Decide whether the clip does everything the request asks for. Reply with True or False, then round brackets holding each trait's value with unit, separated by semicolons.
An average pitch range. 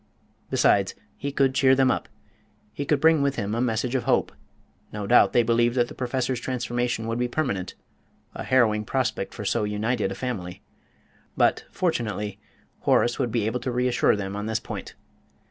True (3.3 semitones)